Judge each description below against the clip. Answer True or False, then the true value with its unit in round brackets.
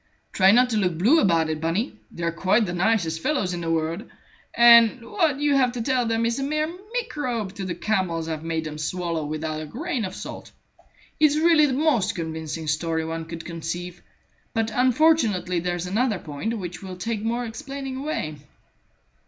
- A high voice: True (195 Hz)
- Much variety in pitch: True (7.3 semitones)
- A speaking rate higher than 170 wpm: True (185 wpm)